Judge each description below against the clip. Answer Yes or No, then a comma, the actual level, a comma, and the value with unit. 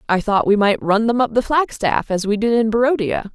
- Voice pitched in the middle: No, high, 220 Hz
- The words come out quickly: Yes, fast, 250 wpm